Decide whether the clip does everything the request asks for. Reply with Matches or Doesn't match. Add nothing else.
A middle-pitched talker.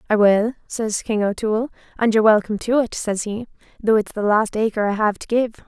Doesn't match